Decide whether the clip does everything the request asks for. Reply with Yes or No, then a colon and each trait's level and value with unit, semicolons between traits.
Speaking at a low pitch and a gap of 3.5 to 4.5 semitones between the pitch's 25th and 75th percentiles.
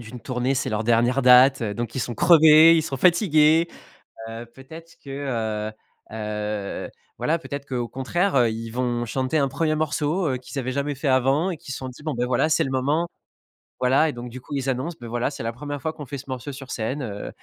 Yes: low, 130 Hz; average, 3.8 semitones